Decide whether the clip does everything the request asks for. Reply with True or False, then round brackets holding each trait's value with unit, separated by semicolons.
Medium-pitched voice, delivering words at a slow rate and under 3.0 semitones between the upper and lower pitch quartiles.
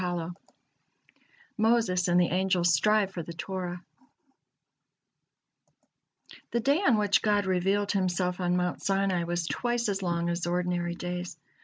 True (180 Hz; 130 wpm; 2.5 semitones)